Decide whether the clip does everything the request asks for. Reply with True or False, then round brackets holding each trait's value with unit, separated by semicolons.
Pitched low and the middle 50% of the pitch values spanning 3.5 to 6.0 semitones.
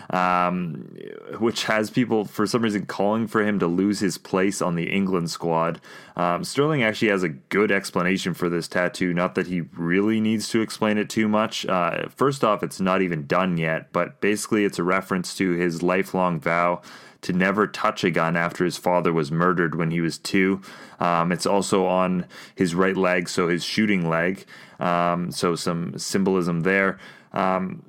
False (90 Hz; 2.5 semitones)